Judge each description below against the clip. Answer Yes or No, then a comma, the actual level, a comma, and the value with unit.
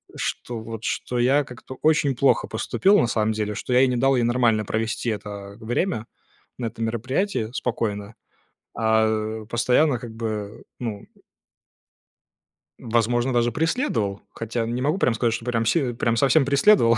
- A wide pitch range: No, narrow, 2.6 semitones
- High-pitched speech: No, low, 120 Hz